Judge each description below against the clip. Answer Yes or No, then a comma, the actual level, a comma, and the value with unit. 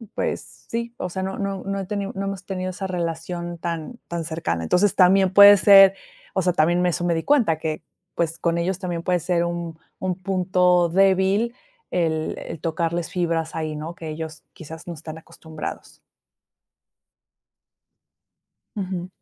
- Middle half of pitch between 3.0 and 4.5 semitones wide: No, narrow, 2.6 semitones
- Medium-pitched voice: Yes, medium, 175 Hz